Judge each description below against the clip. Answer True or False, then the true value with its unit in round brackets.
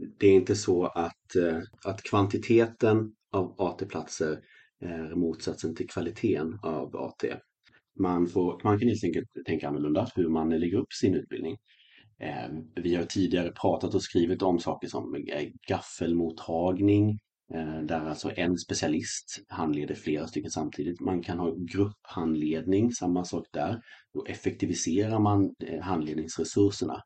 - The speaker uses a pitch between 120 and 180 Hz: False (90 Hz)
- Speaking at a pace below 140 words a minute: True (130 wpm)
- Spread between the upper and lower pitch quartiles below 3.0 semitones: False (3.7 semitones)